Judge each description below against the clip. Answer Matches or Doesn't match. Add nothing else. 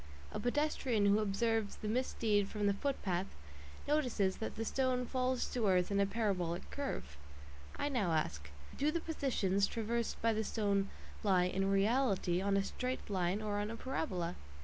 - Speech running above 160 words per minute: Matches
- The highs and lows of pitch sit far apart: Doesn't match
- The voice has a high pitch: Matches